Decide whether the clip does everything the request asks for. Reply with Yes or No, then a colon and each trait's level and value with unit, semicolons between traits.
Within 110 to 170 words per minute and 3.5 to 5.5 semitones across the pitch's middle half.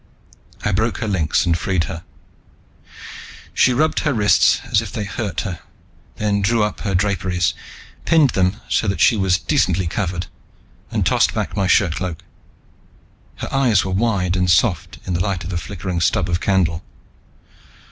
No: average, 165 wpm; average, 3.1 semitones